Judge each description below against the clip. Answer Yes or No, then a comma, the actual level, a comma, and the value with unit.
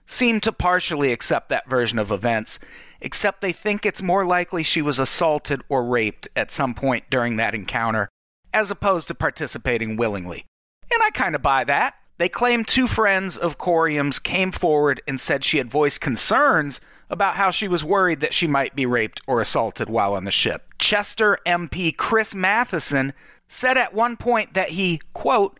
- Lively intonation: Yes, wide, 7.1 semitones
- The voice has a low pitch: No, medium, 170 Hz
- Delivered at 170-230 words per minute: Yes, average, 180 wpm